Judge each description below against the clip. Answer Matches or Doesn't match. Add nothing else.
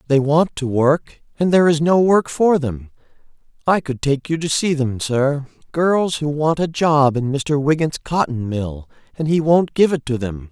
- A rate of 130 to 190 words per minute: Doesn't match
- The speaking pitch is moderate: Matches